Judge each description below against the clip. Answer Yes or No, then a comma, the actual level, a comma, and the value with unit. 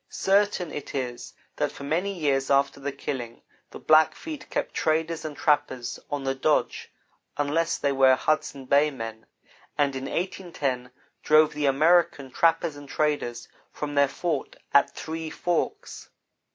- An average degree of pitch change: Yes, average, 3.0 semitones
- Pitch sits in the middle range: Yes, medium, 145 Hz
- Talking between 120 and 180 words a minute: Yes, average, 145 wpm